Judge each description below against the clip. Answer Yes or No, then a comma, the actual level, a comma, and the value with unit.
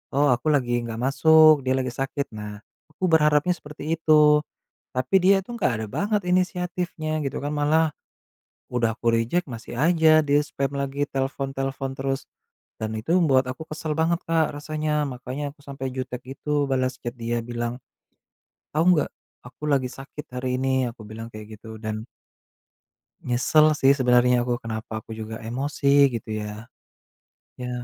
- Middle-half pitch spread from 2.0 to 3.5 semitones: No, average, 3.9 semitones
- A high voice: No, low, 135 Hz